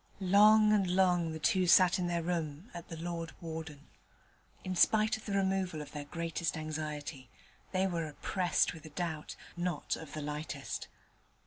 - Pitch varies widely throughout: No, average, 3.0 semitones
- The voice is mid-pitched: Yes, medium, 170 Hz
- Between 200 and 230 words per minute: No, average, 170 wpm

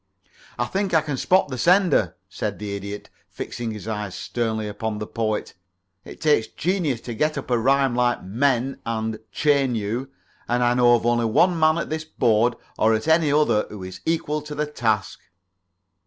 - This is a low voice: Yes, low, 120 Hz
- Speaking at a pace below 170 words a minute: No, average, 185 wpm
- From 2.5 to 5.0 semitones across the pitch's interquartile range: No, wide, 5.4 semitones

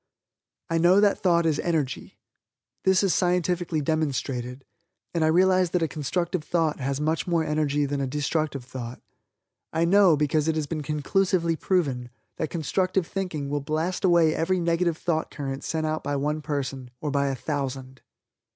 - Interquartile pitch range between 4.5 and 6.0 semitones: No, average, 3.4 semitones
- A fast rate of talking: No, average, 170 wpm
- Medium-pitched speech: Yes, medium, 155 Hz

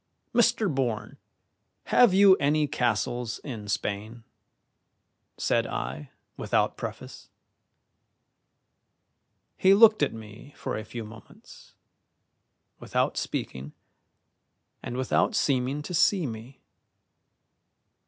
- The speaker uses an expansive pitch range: Yes, wide, 6.1 semitones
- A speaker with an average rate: No, slow, 95 wpm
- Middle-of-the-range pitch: No, low, 125 Hz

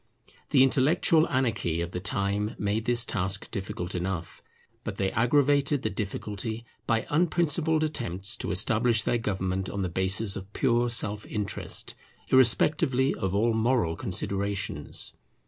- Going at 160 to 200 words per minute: No, slow, 135 wpm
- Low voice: Yes, low, 110 Hz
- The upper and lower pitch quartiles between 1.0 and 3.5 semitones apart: No, average, 4.8 semitones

